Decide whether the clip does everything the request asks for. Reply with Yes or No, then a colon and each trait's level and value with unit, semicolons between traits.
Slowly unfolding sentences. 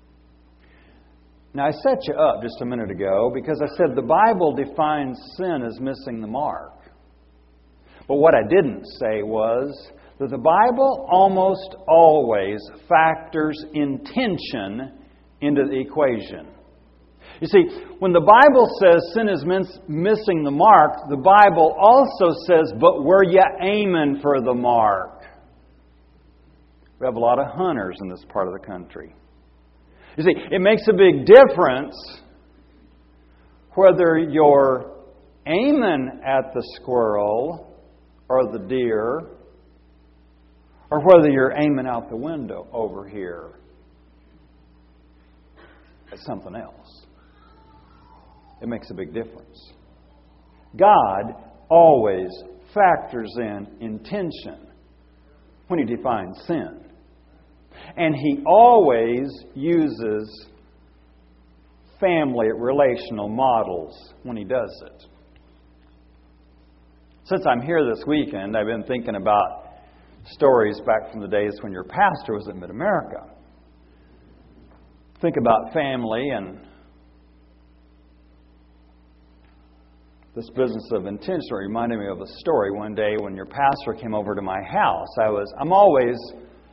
Yes: slow, 120 wpm